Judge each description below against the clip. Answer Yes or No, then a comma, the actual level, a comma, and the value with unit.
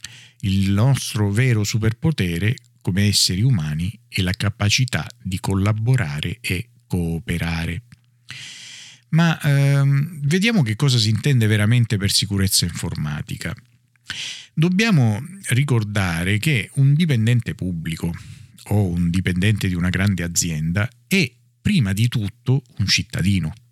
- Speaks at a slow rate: Yes, slow, 110 wpm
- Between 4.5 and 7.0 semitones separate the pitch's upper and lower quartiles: Yes, average, 5.3 semitones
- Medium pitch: No, low, 115 Hz